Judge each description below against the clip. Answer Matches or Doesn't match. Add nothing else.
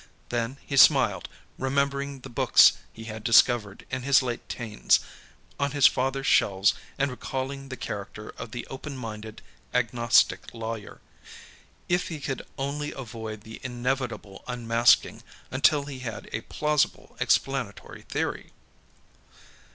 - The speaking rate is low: Matches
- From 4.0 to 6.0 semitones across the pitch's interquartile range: Doesn't match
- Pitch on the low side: Matches